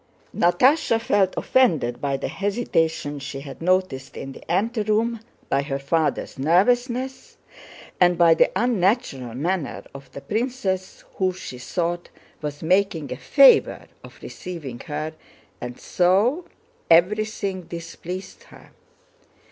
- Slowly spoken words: Yes, slow, 115 wpm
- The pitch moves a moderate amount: No, wide, 6.4 semitones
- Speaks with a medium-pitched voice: Yes, medium, 180 Hz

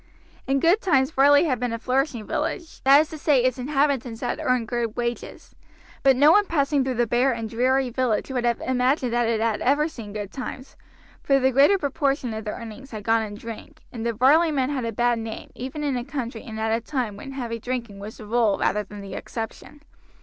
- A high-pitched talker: Yes, very high, 250 Hz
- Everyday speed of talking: No, fast, 225 wpm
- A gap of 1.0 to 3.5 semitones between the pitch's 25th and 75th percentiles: Yes, average, 3.2 semitones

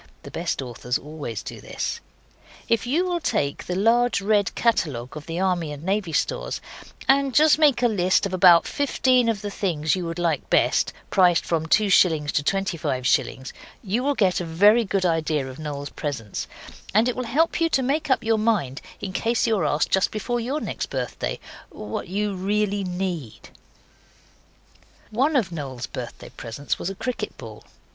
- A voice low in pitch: No, high, 190 Hz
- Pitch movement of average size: No, wide, 6.9 semitones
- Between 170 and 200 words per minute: Yes, average, 180 wpm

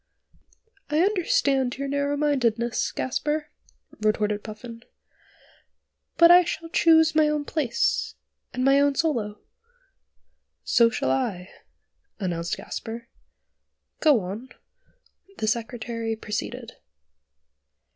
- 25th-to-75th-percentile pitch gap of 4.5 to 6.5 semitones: Yes, wide, 5.5 semitones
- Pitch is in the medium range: No, high, 245 Hz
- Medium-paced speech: No, slow, 95 wpm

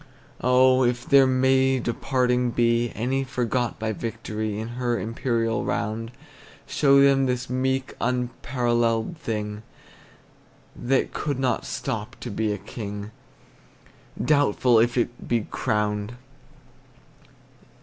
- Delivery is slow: Yes, slow, 110 wpm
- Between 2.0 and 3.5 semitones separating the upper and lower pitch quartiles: Yes, narrow, 2.5 semitones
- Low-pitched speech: Yes, low, 120 Hz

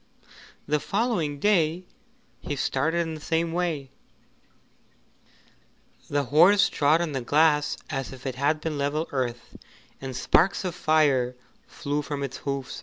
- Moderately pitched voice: Yes, medium, 150 Hz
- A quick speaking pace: No, average, 140 wpm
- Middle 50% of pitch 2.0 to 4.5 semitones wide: Yes, average, 3.0 semitones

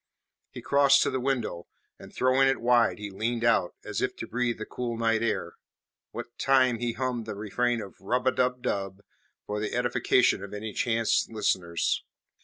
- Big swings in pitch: No, average, 3.0 semitones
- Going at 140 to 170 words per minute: No, average, 185 wpm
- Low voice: Yes, low, 115 Hz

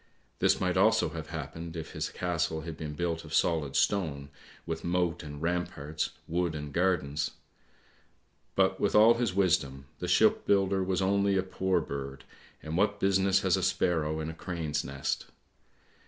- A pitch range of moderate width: Yes, average, 3.6 semitones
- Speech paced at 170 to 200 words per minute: No, average, 160 wpm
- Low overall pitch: Yes, very low, 85 Hz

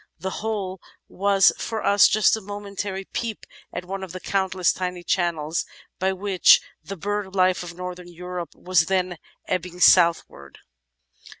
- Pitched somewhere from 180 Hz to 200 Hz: Yes, medium, 185 Hz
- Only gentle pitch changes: Yes, narrow, 1.8 semitones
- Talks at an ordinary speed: Yes, average, 145 wpm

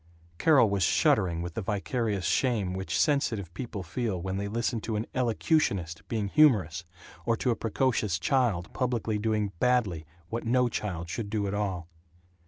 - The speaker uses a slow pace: No, average, 165 wpm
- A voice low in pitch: Yes, low, 105 Hz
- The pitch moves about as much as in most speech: Yes, average, 4.1 semitones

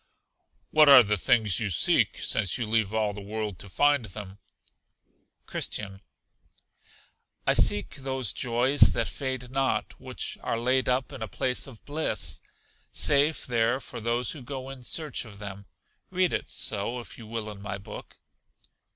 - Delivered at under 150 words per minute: No, average, 160 wpm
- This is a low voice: Yes, low, 115 Hz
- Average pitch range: Yes, average, 4.2 semitones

